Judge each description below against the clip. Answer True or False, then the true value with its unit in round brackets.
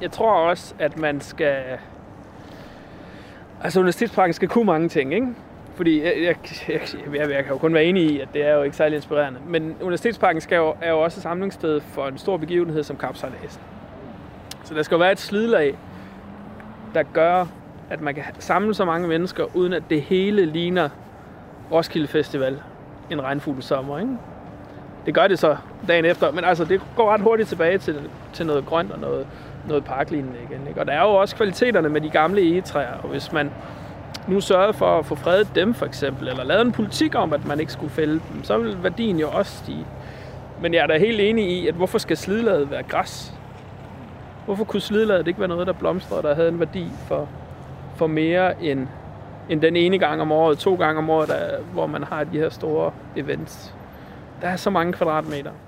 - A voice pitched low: False (160 Hz)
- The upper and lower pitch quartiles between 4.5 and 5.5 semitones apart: False (4.1 semitones)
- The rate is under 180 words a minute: False (200 wpm)